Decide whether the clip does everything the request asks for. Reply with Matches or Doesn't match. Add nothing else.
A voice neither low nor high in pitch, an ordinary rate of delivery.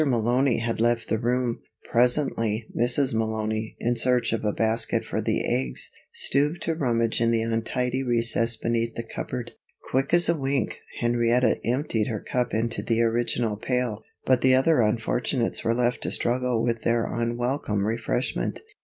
Doesn't match